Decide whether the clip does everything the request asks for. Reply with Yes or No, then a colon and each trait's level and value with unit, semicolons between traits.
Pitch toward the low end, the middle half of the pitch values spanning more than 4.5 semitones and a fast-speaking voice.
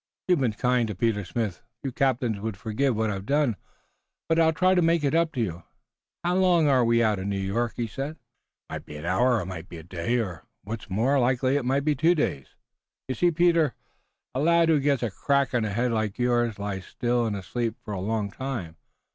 Yes: low, 120 Hz; wide, 5.4 semitones; fast, 230 wpm